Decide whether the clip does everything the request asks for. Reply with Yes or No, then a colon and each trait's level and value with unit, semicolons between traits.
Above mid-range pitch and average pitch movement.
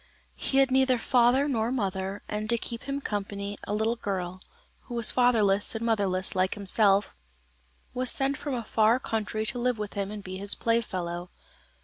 Yes: high, 220 Hz; average, 3.6 semitones